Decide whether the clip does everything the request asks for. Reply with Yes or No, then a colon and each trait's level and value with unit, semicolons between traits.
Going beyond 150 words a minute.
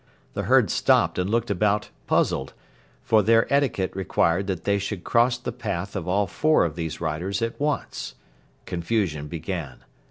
Yes: average, 160 wpm